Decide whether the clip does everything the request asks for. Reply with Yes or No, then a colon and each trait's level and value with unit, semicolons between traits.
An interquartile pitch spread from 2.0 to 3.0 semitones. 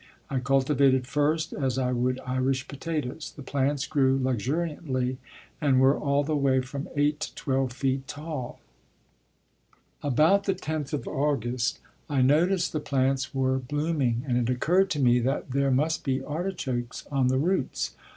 Yes: narrow, 2.5 semitones